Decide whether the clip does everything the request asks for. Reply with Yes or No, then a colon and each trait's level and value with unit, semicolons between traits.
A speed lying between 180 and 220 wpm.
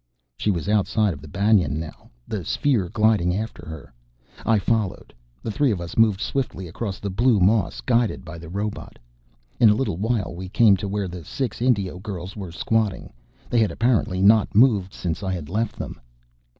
Yes: average, 190 wpm